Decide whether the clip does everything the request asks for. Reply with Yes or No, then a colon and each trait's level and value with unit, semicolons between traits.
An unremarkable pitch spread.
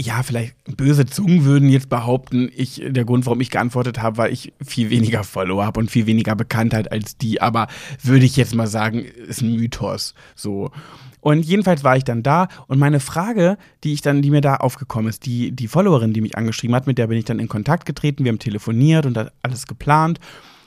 Yes: average, 3.9 semitones